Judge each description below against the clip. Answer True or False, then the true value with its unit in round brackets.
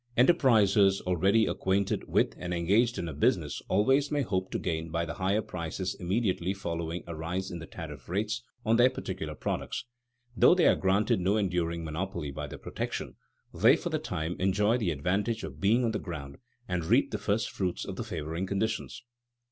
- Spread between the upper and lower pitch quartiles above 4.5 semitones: False (4.2 semitones)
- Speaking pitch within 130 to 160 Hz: False (95 Hz)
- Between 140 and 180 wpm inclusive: False (190 wpm)